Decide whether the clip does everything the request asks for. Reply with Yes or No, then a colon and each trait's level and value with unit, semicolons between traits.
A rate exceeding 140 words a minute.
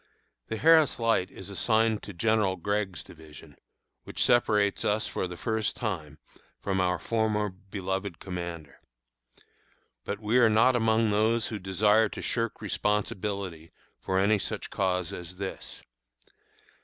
No: slow, 135 wpm